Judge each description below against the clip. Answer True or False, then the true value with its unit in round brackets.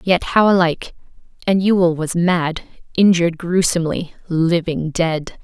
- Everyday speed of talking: False (120 wpm)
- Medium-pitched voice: True (170 Hz)